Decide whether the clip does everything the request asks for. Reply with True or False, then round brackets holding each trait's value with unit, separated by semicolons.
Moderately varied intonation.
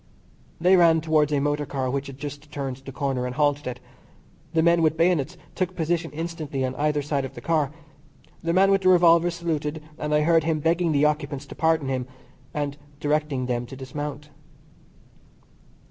True (3.0 semitones)